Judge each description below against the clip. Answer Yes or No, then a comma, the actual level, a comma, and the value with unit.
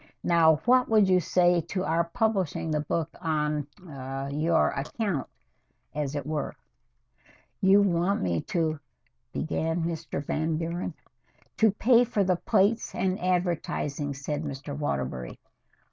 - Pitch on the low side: No, medium, 165 Hz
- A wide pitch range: No, average, 4.0 semitones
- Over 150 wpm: No, slow, 135 wpm